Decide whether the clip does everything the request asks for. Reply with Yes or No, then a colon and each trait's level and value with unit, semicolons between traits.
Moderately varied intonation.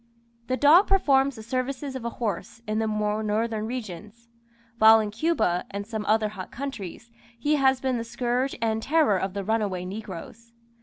Yes: average, 3.5 semitones